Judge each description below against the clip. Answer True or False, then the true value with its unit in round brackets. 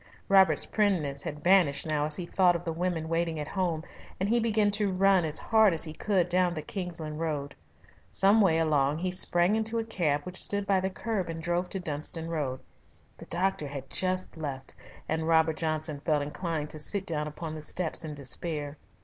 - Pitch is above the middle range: False (165 Hz)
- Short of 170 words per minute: False (200 wpm)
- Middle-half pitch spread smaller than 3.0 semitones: False (3.6 semitones)